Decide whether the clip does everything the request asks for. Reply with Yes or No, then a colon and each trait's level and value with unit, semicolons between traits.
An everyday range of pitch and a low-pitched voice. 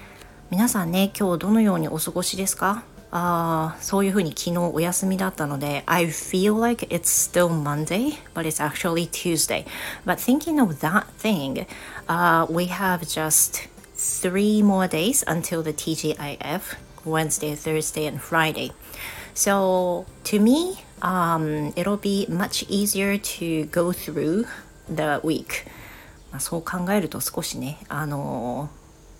No: average, 4.1 semitones; medium, 175 Hz